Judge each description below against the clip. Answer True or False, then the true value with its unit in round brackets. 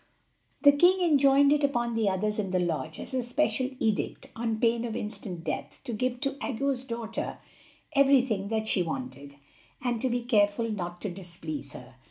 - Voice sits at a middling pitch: False (230 Hz)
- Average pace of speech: True (180 wpm)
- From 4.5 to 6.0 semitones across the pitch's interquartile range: True (4.9 semitones)